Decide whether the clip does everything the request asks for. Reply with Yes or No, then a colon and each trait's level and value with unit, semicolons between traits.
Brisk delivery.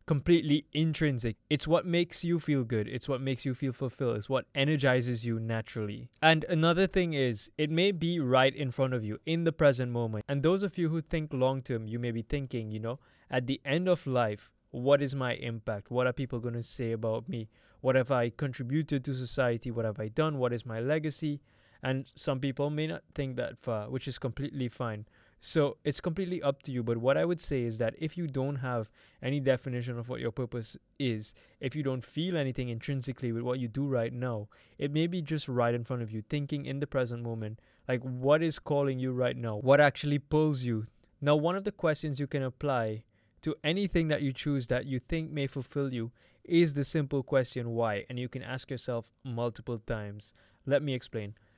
Yes: fast, 220 wpm